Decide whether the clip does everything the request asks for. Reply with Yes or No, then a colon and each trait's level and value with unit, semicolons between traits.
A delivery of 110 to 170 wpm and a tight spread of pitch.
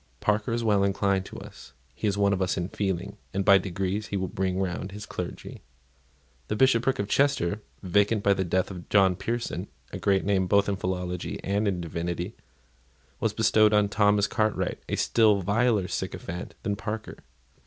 No: average, 180 wpm; narrow, 2.2 semitones